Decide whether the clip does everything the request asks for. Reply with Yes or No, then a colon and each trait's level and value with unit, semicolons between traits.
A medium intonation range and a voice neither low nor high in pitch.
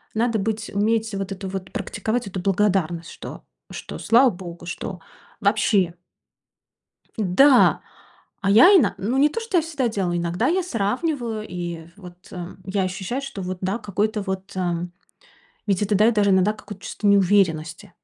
No: average, 3.5 semitones; high, 200 Hz